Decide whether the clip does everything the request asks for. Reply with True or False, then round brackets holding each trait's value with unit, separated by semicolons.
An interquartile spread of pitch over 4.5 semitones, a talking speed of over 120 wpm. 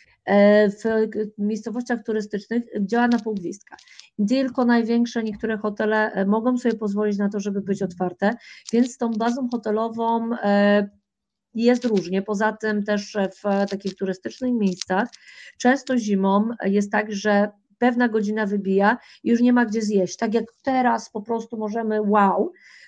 False (2.4 semitones; 135 wpm)